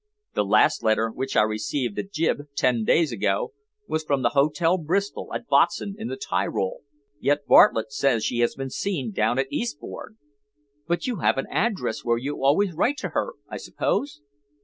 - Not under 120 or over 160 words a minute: No, average, 180 wpm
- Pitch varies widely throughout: Yes, wide, 7.0 semitones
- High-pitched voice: No, medium, 140 Hz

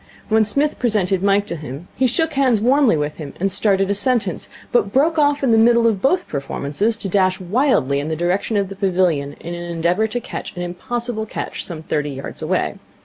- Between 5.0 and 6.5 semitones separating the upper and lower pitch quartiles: Yes, wide, 5.6 semitones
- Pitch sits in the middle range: No, high, 200 Hz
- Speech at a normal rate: No, fast, 210 wpm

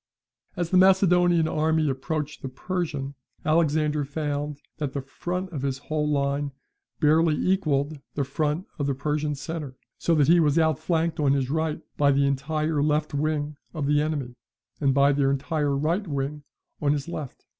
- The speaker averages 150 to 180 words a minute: Yes, average, 165 wpm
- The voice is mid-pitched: Yes, medium, 150 Hz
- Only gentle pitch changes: Yes, narrow, 2.2 semitones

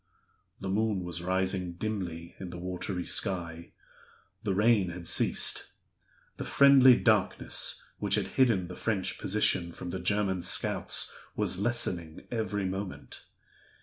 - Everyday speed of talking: No, slow, 130 wpm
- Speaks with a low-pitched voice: Yes, very low, 95 Hz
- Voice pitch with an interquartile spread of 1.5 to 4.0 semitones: Yes, average, 3.0 semitones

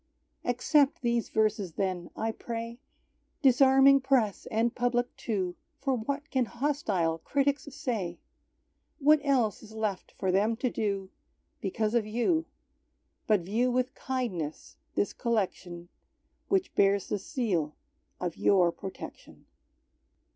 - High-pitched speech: Yes, high, 225 Hz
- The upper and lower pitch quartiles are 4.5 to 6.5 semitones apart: Yes, average, 5.1 semitones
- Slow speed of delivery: Yes, slow, 120 wpm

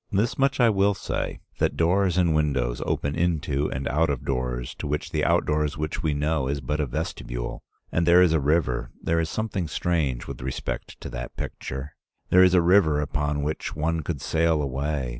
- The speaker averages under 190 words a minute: No, average, 195 wpm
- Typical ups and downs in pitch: Yes, average, 3.5 semitones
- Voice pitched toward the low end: Yes, very low, 75 Hz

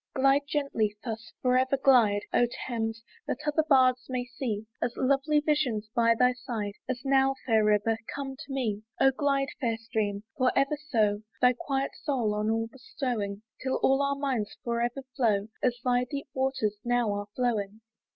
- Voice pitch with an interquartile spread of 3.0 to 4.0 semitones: Yes, average, 3.4 semitones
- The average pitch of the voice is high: Yes, very high, 250 Hz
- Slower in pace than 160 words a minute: No, average, 175 wpm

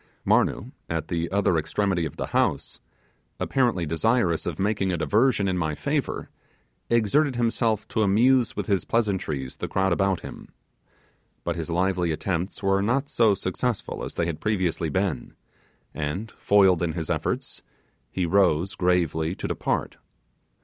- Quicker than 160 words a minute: No, average, 150 wpm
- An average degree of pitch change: Yes, average, 4.2 semitones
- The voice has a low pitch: Yes, very low, 95 Hz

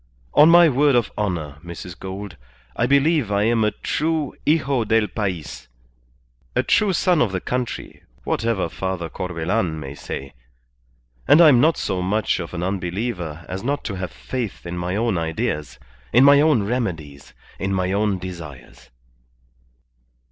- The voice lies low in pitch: Yes, low, 100 Hz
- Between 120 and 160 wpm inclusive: Yes, average, 155 wpm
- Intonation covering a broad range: Yes, wide, 6.2 semitones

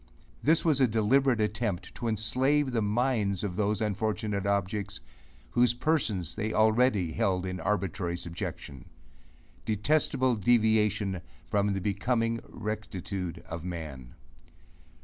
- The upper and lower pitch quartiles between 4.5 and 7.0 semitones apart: No, average, 3.6 semitones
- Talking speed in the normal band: No, slow, 115 wpm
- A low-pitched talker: Yes, low, 105 Hz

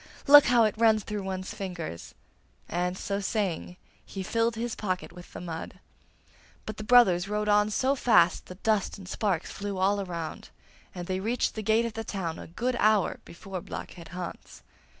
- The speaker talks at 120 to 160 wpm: No, average, 180 wpm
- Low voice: No, high, 200 Hz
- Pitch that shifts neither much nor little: Yes, average, 3.4 semitones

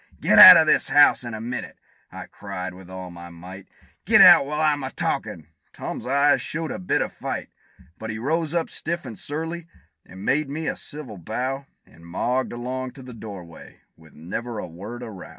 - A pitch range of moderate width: No, wide, 7.7 semitones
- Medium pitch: No, low, 120 Hz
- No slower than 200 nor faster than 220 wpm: Yes, fast, 205 wpm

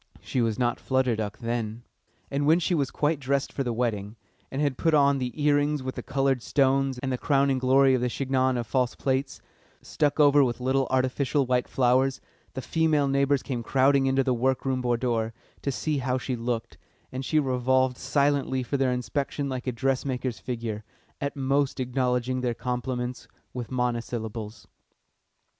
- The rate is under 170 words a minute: No, average, 175 wpm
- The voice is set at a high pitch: No, low, 130 Hz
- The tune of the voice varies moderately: No, narrow, 1.9 semitones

